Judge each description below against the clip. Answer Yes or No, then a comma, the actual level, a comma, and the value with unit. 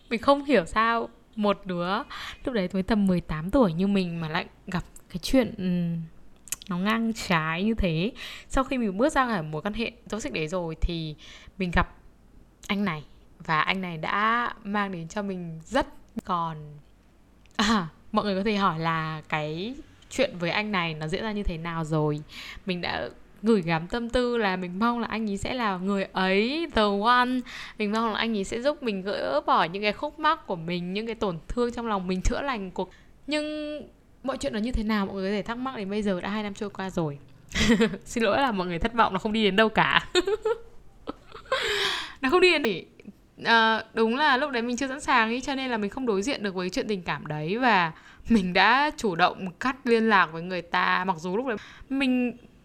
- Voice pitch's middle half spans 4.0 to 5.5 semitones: Yes, average, 4.7 semitones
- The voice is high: Yes, high, 210 Hz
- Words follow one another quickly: No, average, 220 wpm